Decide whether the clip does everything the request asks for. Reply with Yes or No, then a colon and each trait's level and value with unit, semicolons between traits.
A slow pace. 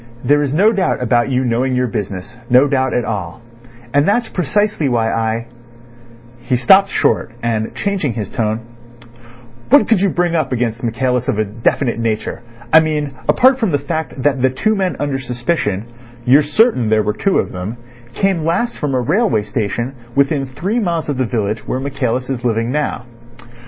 No: average, 175 wpm